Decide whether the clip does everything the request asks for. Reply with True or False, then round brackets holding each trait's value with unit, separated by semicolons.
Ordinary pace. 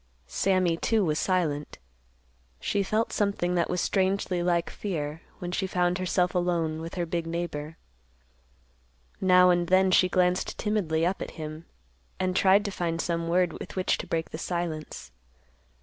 True (160 wpm)